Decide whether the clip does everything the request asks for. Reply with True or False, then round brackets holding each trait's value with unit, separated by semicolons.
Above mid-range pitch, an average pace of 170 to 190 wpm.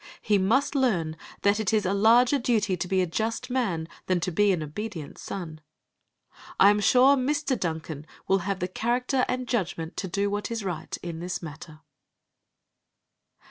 True (200 Hz; 175 wpm)